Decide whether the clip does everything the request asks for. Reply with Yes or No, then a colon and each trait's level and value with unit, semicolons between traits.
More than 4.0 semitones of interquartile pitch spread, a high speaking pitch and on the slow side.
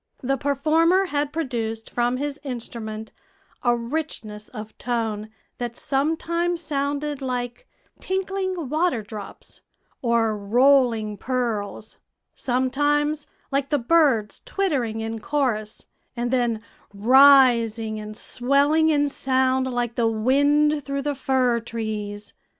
Yes: average, 4.4 semitones; very high, 255 Hz; slow, 110 wpm